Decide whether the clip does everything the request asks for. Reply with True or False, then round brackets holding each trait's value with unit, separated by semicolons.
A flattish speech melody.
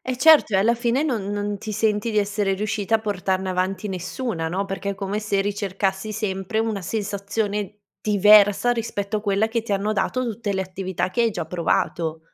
True (2.2 semitones)